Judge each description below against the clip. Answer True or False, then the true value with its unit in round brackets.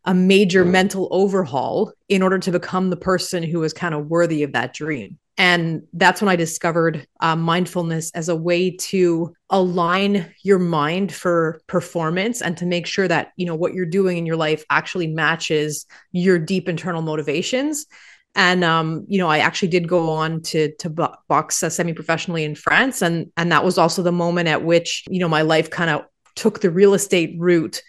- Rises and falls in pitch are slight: True (2.3 semitones)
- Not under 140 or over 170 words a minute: False (190 wpm)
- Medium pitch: True (175 Hz)